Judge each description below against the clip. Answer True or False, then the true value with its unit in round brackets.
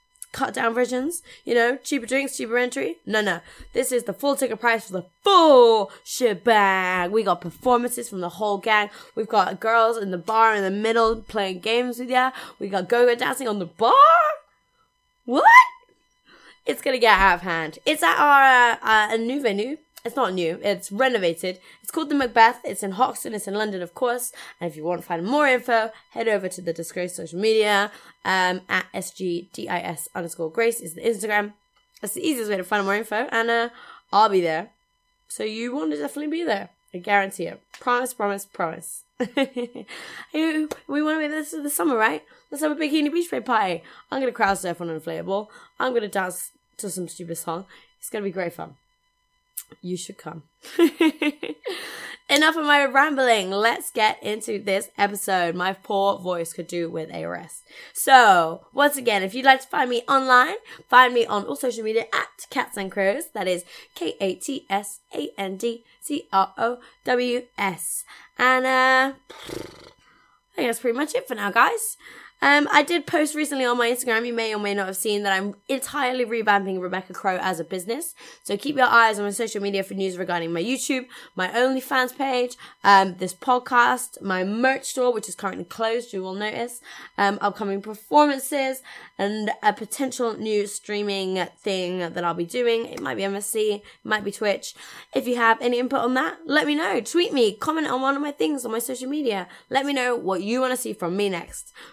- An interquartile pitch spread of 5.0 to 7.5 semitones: True (5.3 semitones)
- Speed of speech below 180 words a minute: False (200 wpm)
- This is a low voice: False (225 Hz)